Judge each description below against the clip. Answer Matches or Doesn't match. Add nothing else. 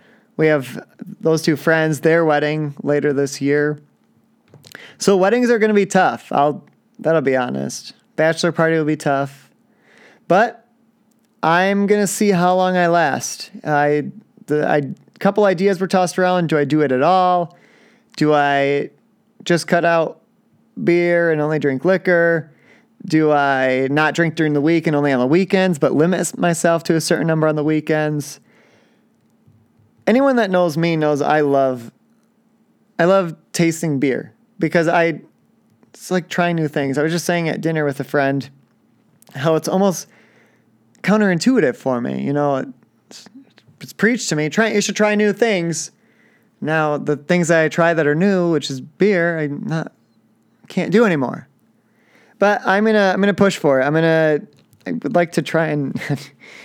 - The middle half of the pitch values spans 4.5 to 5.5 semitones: Matches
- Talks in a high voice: Doesn't match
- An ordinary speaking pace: Matches